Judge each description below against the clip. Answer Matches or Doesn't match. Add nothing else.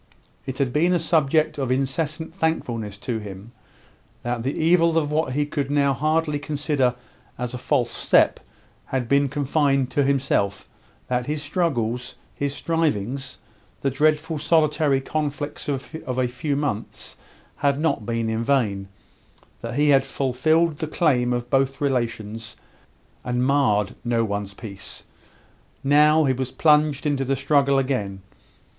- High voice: Doesn't match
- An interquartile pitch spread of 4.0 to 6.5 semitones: Doesn't match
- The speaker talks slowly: Doesn't match